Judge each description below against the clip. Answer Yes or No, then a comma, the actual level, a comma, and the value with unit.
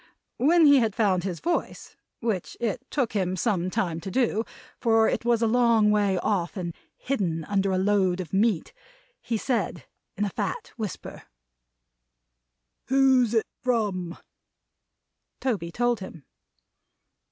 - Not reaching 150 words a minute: Yes, average, 140 wpm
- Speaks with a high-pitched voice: Yes, high, 210 Hz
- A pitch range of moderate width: Yes, average, 4.4 semitones